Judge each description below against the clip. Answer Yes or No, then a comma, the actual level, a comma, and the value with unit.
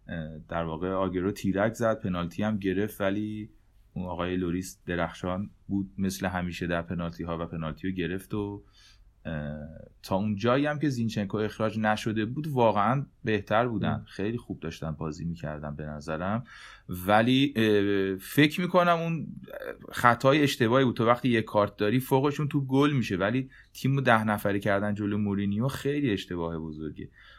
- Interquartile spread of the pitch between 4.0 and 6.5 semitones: Yes, average, 4.4 semitones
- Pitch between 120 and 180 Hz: No, low, 105 Hz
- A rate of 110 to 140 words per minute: No, fast, 155 wpm